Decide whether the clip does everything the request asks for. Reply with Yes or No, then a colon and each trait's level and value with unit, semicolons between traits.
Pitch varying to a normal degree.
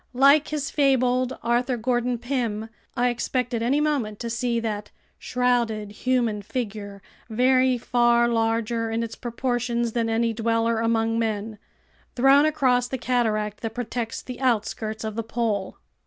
No: narrow, 1.9 semitones